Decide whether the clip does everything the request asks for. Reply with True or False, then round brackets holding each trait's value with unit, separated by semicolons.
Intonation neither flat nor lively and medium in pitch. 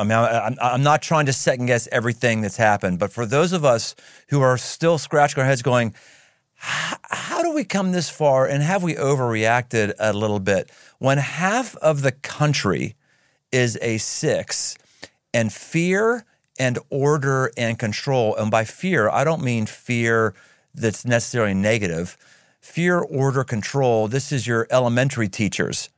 False (4.5 semitones; 130 Hz)